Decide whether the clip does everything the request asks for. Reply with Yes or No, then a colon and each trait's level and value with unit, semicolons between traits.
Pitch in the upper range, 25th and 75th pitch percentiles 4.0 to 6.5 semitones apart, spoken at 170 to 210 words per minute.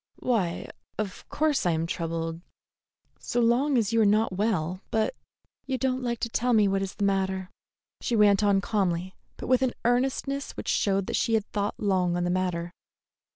Yes: high, 205 Hz; average, 4.4 semitones; average, 190 wpm